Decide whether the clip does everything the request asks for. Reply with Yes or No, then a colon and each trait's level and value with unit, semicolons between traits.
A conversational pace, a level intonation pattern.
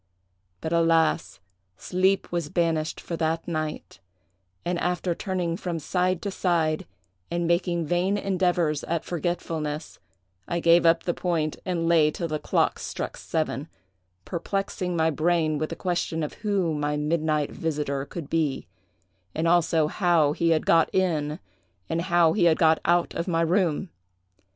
Yes: average, 150 wpm; narrow, 2.0 semitones